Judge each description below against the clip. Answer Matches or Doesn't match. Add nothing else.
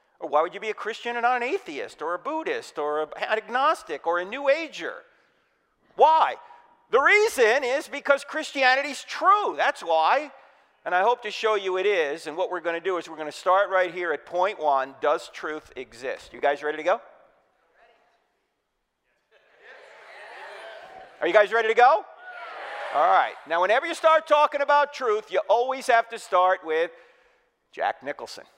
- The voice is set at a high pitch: Matches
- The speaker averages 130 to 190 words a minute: Matches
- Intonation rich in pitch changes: Matches